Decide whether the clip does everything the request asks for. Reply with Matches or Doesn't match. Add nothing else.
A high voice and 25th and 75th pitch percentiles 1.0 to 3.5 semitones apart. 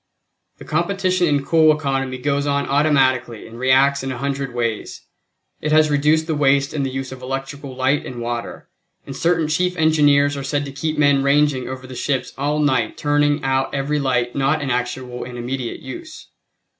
Doesn't match